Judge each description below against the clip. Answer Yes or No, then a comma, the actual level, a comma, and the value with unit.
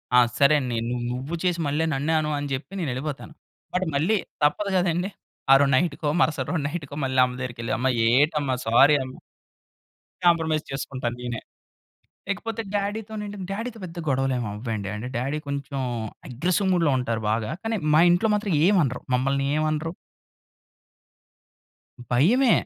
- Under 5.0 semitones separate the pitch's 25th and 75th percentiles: No, wide, 5.4 semitones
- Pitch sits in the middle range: Yes, medium, 150 Hz